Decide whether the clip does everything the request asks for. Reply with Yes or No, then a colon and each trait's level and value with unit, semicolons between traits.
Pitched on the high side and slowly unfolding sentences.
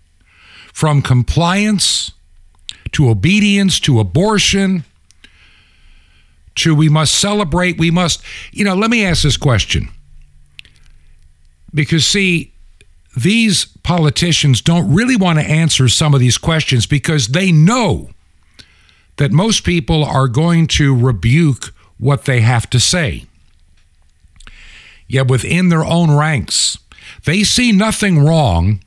No: low, 135 Hz; slow, 115 wpm